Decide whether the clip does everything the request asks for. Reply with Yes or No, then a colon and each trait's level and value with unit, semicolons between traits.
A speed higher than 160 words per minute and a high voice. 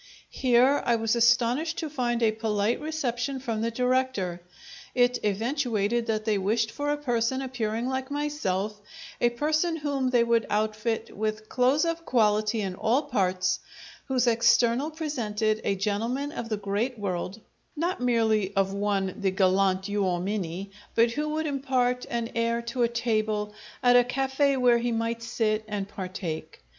No: average, 155 wpm; high, 230 Hz